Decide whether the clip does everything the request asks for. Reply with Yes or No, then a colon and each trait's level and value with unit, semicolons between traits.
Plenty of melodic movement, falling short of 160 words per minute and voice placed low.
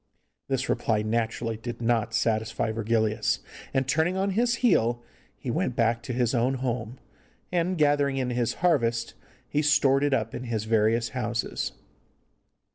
No: average, 3.5 semitones; average, 150 wpm; low, 120 Hz